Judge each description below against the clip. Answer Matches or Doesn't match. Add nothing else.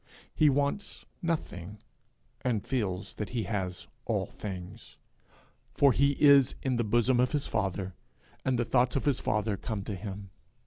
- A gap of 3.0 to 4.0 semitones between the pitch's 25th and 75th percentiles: Doesn't match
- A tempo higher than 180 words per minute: Doesn't match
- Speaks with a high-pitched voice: Doesn't match